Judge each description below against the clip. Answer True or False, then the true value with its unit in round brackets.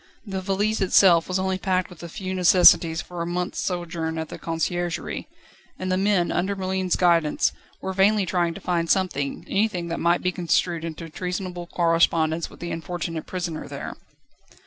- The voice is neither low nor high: True (175 Hz)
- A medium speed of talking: True (170 wpm)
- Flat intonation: True (1.9 semitones)